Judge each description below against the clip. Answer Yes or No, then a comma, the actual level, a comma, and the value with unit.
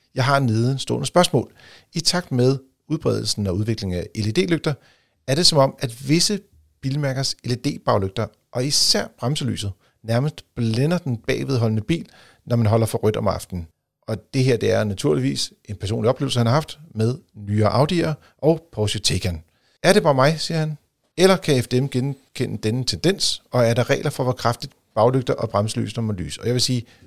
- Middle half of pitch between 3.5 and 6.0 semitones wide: Yes, average, 4.3 semitones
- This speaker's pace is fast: No, average, 185 wpm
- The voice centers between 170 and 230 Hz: No, low, 125 Hz